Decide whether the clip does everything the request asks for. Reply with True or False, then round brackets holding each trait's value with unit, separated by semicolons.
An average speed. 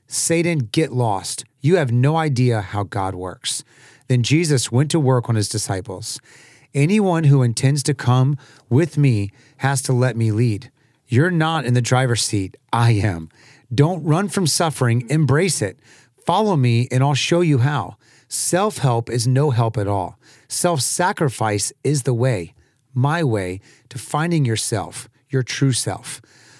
True (160 wpm)